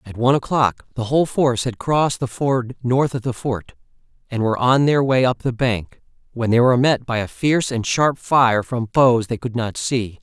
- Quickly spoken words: Yes, fast, 225 wpm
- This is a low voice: Yes, low, 125 Hz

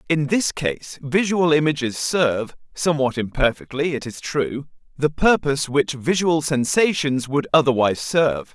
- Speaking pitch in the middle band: Yes, medium, 145 Hz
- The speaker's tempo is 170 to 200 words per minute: No, slow, 135 wpm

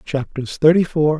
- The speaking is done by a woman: No, male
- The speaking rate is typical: Yes, average, 150 wpm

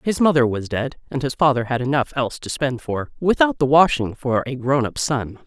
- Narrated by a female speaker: Yes, female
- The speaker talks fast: Yes, fast, 230 wpm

